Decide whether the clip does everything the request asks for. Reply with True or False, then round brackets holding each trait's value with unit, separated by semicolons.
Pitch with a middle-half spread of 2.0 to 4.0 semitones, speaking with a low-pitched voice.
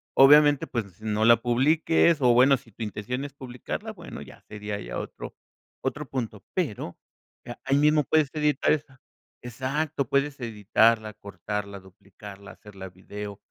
False (5.2 semitones; 120 Hz)